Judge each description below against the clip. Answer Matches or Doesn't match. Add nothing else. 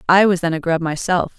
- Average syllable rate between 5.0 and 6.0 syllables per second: Matches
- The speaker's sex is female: Matches